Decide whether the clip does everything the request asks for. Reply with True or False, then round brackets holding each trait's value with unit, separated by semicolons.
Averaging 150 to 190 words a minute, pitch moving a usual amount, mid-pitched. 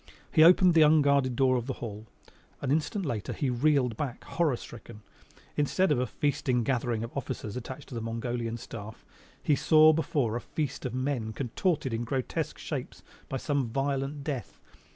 False (170 wpm; 3.8 semitones; 130 Hz)